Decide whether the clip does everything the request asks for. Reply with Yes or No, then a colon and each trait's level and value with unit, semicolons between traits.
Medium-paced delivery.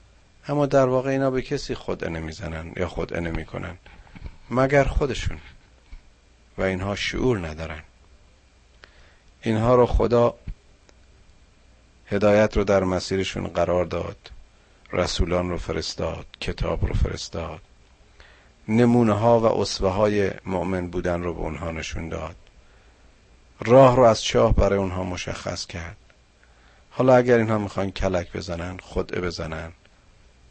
Yes: average, 120 wpm